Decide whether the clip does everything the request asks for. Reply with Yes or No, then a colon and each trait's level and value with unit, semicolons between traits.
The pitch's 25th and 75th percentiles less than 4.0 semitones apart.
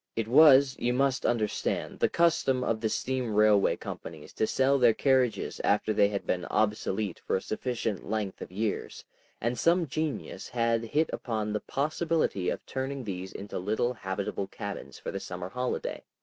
No: average, 4.3 semitones